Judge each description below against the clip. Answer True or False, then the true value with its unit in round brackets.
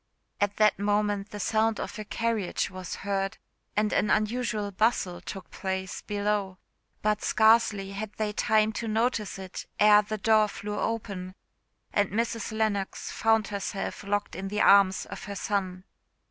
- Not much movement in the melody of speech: True (1.7 semitones)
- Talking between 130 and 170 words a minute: True (155 wpm)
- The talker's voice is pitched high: True (210 Hz)